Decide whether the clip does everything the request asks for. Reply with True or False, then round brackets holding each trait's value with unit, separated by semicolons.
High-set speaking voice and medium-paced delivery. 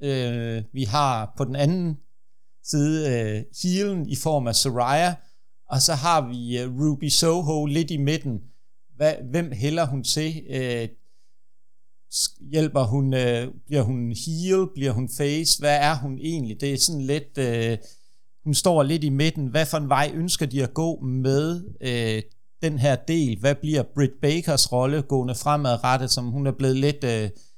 False (140 Hz; 170 wpm)